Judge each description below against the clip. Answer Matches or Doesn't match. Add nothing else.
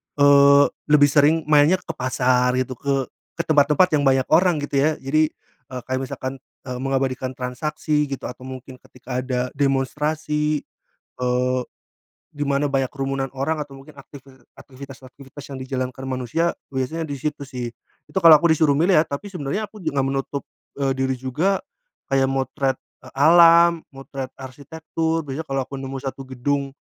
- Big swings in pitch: Doesn't match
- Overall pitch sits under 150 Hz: Matches